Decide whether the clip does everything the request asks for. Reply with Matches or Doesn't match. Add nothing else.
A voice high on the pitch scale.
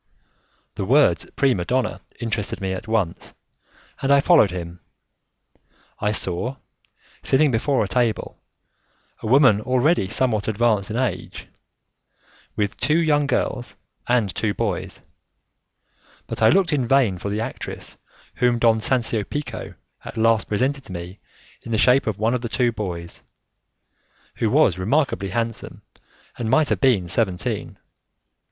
Doesn't match